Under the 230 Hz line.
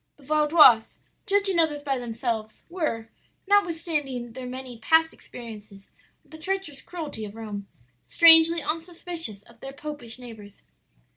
No: very high, 275 Hz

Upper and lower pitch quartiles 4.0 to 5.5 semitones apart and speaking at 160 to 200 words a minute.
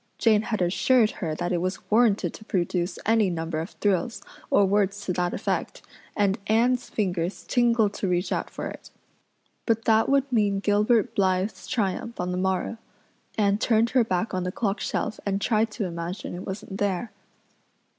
No: average, 3.5 semitones; average, 175 wpm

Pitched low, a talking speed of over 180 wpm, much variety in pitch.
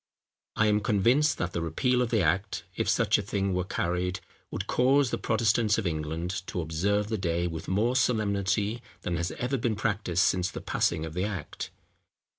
No: low, 100 Hz; average, 190 wpm; average, 4.2 semitones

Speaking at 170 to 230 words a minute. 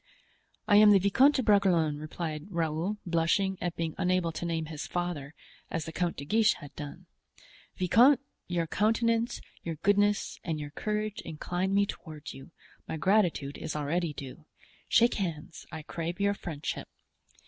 No: average, 155 wpm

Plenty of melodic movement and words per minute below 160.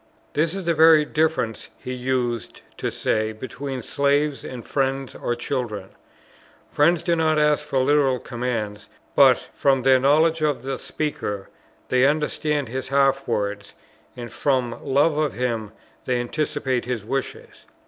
No: average, 3.6 semitones; average, 145 wpm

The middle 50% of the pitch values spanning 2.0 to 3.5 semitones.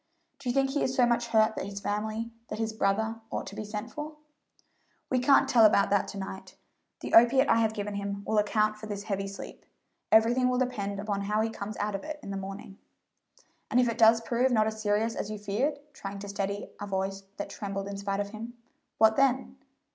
Yes: average, 2.7 semitones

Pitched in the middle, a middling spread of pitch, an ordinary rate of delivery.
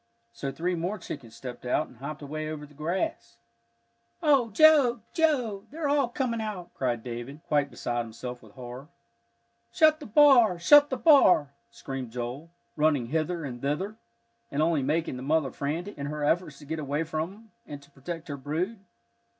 No: medium, 155 Hz; wide, 7.2 semitones; average, 175 wpm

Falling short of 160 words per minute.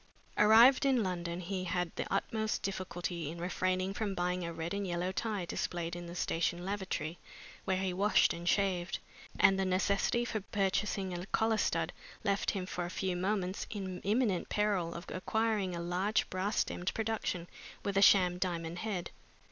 No: average, 170 wpm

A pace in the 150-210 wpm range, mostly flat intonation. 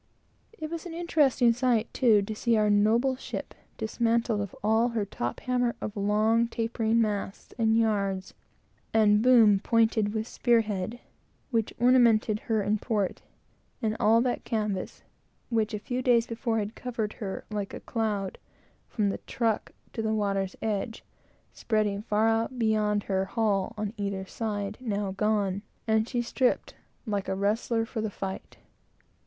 Yes: average, 155 wpm; narrow, 2.1 semitones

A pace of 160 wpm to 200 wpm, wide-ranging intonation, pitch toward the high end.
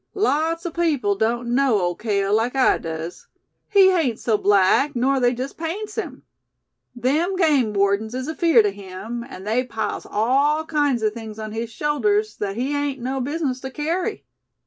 Yes: average, 175 wpm; wide, 5.7 semitones; very high, 250 Hz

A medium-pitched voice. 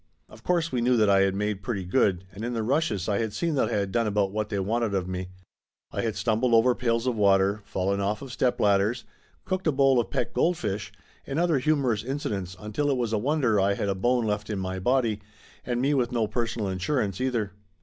No: low, 110 Hz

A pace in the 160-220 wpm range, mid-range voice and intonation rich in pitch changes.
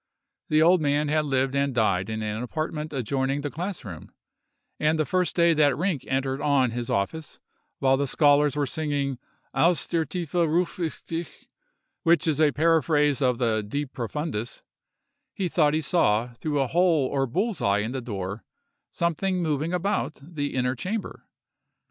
No: average, 170 wpm; medium, 145 Hz; average, 4.1 semitones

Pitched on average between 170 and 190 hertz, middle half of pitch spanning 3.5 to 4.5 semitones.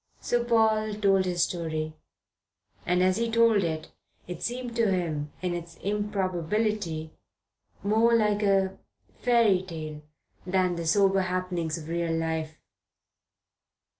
Yes: medium, 185 Hz; average, 4.2 semitones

